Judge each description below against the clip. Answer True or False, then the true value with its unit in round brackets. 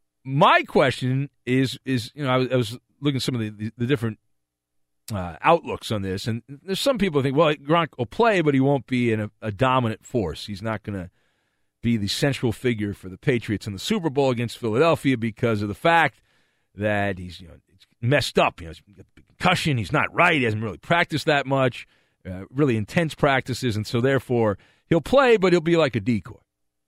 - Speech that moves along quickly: True (210 wpm)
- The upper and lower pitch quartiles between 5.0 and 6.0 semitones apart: True (5.4 semitones)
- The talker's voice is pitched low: True (120 Hz)